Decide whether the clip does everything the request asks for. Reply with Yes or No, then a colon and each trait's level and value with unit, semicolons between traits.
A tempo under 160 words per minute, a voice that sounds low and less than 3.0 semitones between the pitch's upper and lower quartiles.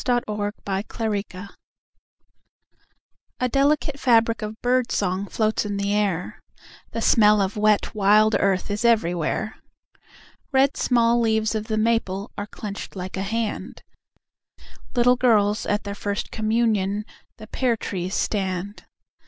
No: average, 140 wpm; high, 215 Hz; narrow, 2.4 semitones